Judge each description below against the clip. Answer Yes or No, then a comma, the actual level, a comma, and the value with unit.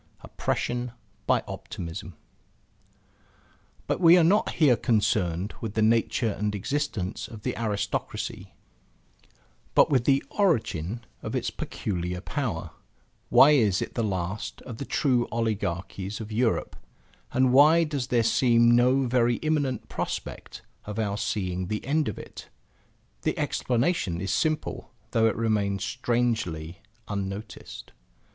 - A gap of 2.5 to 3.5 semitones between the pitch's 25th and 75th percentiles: No, average, 4.3 semitones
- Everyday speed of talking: No, slow, 130 wpm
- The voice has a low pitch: Yes, low, 115 Hz